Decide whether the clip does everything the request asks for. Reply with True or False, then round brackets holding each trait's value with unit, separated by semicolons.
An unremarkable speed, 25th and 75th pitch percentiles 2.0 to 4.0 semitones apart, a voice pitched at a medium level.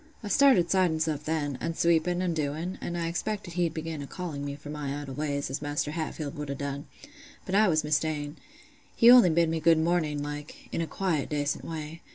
False (210 wpm; 2.7 semitones; 160 Hz)